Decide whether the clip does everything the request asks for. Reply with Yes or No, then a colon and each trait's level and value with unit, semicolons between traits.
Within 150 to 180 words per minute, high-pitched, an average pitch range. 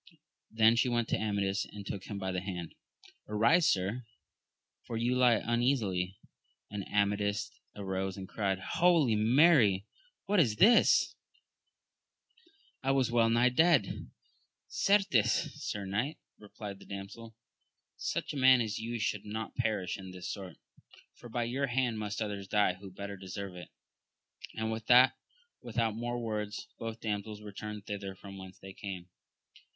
No: average, 155 wpm; low, 105 Hz; average, 3.4 semitones